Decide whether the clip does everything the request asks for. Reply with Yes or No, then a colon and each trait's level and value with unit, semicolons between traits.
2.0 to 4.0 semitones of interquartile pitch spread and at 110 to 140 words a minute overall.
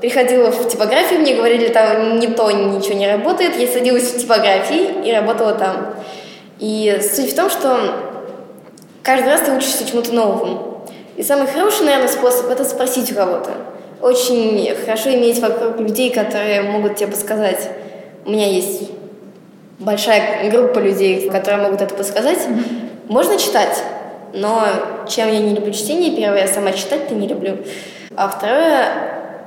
No: average, 3.4 semitones; average, 150 wpm